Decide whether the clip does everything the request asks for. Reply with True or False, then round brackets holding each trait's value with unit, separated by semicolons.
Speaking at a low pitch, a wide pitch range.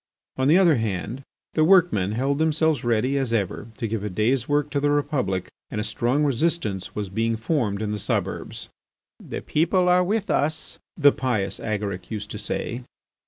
True (125 Hz; 6.1 semitones)